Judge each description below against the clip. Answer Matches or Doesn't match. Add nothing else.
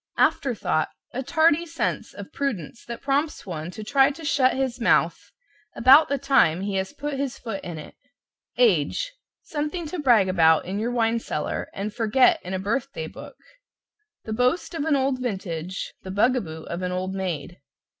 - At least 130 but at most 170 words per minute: Doesn't match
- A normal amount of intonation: Doesn't match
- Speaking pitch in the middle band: Doesn't match